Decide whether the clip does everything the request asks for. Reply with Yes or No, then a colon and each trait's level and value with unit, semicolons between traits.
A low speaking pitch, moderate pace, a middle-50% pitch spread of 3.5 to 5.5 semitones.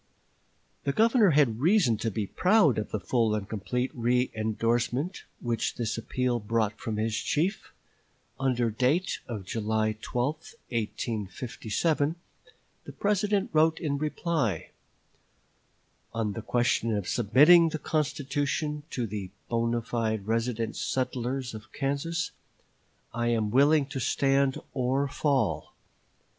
No: low, 125 Hz; slow, 125 wpm; average, 4.7 semitones